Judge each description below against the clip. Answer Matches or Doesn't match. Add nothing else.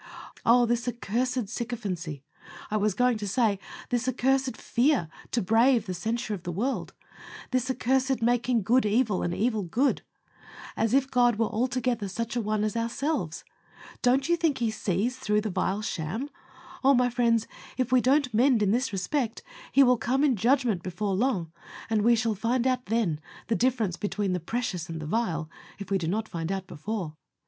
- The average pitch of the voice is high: Matches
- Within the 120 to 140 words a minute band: Doesn't match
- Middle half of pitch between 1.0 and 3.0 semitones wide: Doesn't match